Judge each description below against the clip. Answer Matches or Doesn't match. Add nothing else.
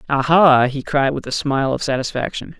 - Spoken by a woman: Doesn't match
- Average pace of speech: Matches